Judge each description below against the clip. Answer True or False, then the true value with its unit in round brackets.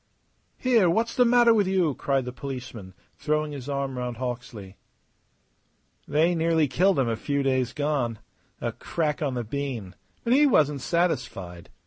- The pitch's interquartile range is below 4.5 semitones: False (5.4 semitones)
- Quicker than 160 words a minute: False (155 wpm)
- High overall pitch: False (140 Hz)